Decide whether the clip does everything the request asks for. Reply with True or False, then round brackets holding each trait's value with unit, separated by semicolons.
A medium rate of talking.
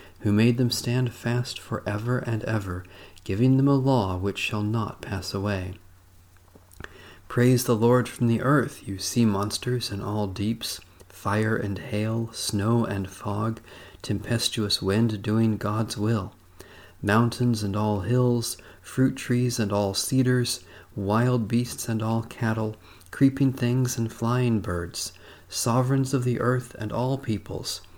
True (145 wpm)